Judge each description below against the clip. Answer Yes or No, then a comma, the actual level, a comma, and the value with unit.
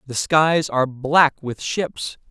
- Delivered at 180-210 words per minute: No, average, 155 wpm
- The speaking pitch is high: No, medium, 145 Hz